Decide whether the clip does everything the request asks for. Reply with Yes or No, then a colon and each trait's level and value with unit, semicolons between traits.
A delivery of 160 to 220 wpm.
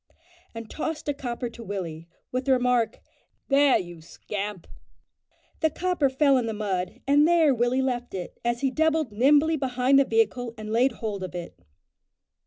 Yes: average, 170 wpm